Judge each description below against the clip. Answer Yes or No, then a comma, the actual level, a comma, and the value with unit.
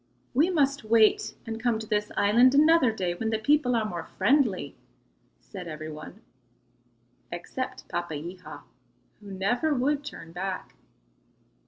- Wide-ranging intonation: Yes, wide, 6.2 semitones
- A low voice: No, high, 220 Hz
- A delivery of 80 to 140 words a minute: Yes, slow, 135 wpm